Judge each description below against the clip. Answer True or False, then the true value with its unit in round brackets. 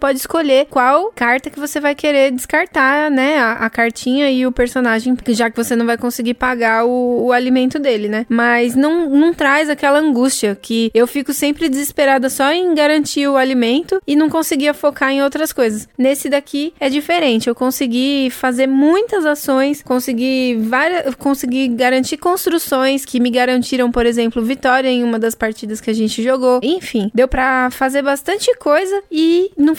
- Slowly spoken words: False (175 wpm)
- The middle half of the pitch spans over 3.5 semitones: False (3.1 semitones)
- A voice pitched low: False (265 Hz)